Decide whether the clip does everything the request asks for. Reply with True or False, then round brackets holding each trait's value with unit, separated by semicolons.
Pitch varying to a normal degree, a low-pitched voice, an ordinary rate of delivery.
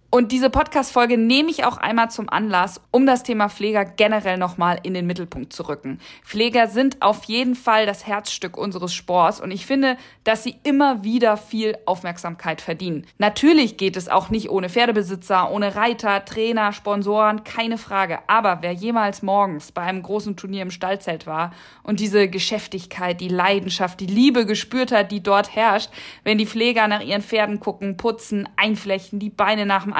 False (3.2 semitones; 205 Hz; 175 wpm)